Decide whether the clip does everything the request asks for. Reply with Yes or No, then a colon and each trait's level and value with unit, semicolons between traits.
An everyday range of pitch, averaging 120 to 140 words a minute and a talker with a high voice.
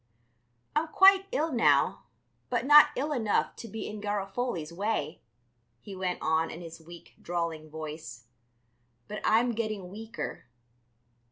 No: wide, 6.2 semitones; slow, 135 wpm; high, 205 Hz